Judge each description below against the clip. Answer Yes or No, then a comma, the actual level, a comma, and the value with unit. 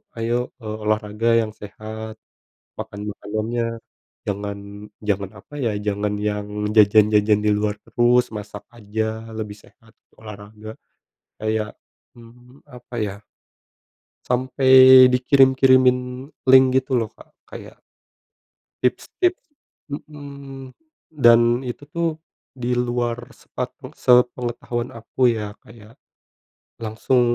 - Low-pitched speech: Yes, low, 115 Hz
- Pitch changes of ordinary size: Yes, average, 3.0 semitones